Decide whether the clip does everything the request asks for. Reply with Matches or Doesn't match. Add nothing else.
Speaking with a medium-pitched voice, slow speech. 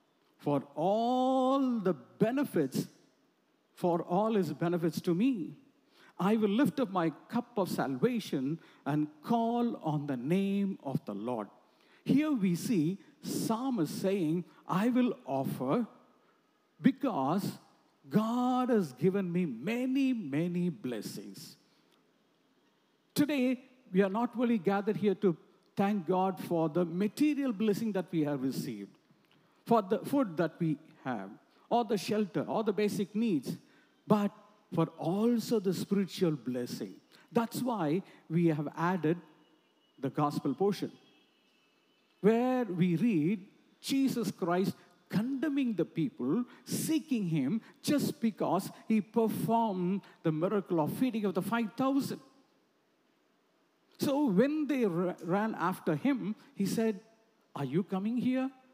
Doesn't match